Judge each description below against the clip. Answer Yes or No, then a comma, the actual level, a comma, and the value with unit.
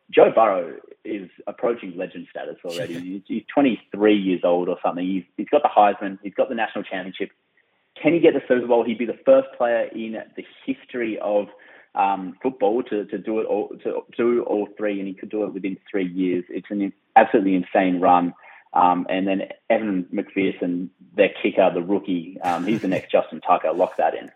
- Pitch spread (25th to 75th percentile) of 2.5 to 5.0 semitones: Yes, average, 4.0 semitones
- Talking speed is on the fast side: No, average, 195 wpm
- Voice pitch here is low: Yes, low, 105 Hz